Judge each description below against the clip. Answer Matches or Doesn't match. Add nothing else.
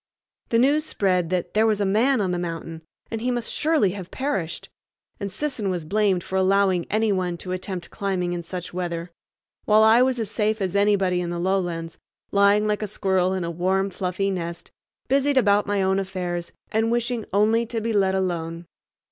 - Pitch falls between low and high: Doesn't match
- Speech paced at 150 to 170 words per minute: Doesn't match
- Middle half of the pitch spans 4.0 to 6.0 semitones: Doesn't match